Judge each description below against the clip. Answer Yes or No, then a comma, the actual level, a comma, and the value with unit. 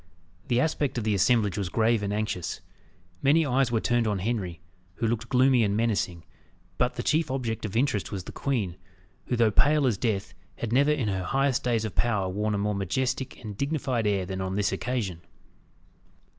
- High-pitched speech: No, low, 115 Hz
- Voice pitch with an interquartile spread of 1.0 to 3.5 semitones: No, average, 4.2 semitones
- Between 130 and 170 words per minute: No, average, 195 wpm